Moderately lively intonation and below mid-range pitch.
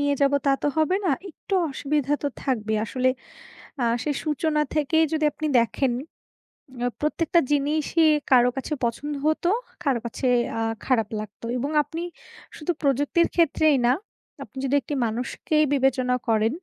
No: average, 3.5 semitones; very high, 285 Hz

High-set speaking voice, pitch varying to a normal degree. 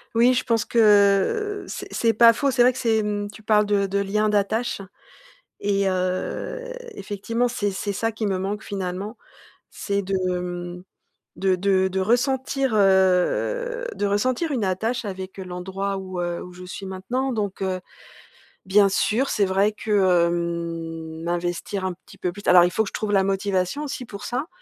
Yes: high, 200 Hz; average, 3.3 semitones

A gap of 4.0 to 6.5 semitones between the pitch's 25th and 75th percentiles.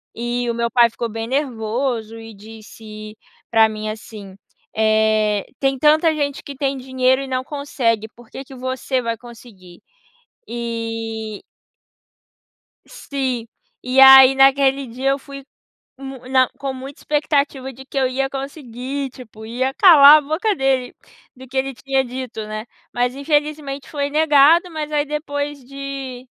No: average, 3.3 semitones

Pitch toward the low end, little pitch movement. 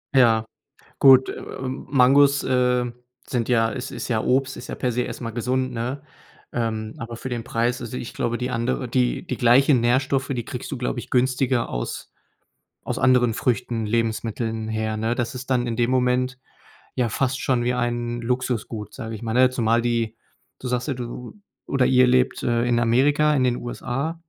Yes: low, 125 Hz; narrow, 1.8 semitones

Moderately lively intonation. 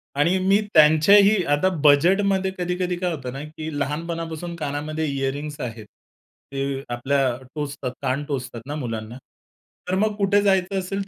Yes: average, 4.9 semitones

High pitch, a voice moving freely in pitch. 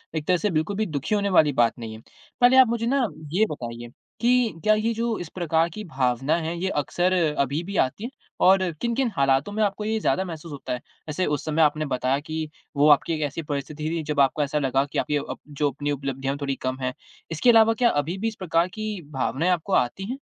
No: medium, 160 Hz; wide, 6.6 semitones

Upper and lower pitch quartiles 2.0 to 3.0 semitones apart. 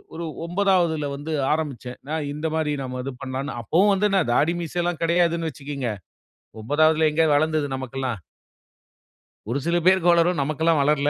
No: average, 3.4 semitones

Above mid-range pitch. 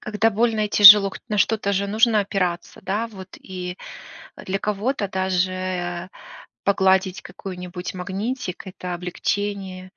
Yes: high, 195 Hz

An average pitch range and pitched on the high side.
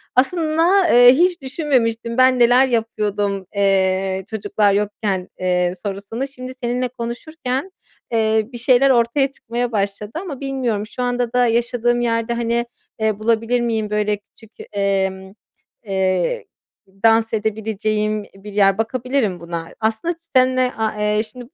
Yes: average, 3.4 semitones; high, 230 Hz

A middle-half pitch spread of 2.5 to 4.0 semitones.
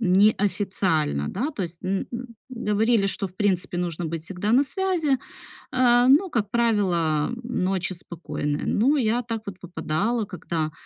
No: average, 5.3 semitones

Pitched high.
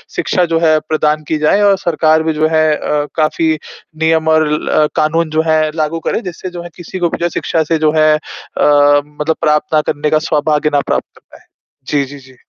No: medium, 155 Hz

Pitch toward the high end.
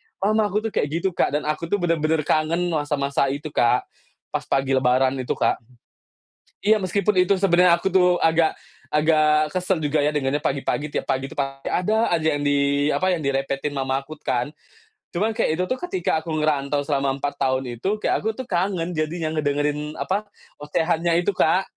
No: medium, 155 Hz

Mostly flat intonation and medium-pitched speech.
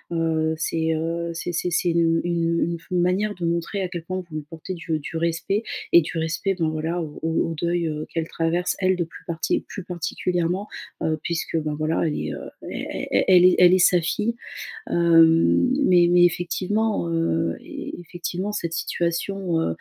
Yes: narrow, 1.6 semitones; medium, 170 Hz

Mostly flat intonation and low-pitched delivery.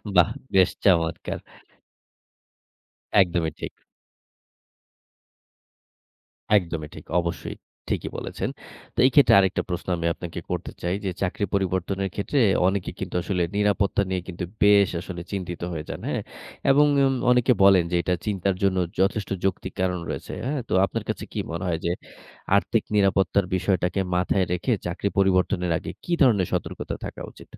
Yes: narrow, 2.2 semitones; very low, 95 Hz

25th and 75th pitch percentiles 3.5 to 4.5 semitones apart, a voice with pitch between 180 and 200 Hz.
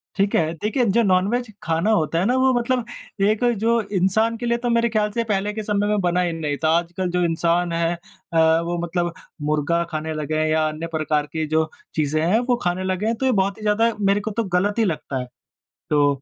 No: average, 4.9 semitones; medium, 185 Hz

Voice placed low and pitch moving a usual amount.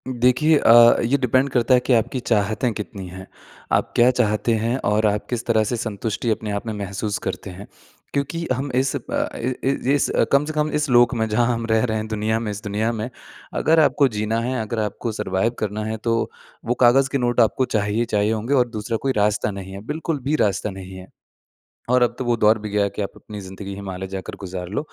Yes: low, 110 Hz; average, 3.1 semitones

